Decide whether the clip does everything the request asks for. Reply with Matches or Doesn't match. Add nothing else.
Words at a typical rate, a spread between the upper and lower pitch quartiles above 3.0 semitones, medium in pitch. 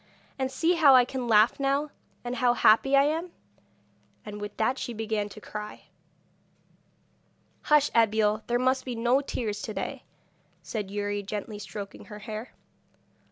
Doesn't match